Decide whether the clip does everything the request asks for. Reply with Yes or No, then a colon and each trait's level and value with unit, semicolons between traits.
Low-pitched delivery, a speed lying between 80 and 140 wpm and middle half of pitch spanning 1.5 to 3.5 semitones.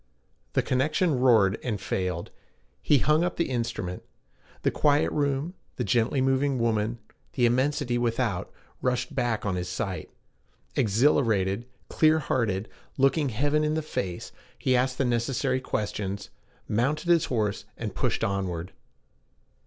No: low, 125 Hz; slow, 135 wpm; average, 5.2 semitones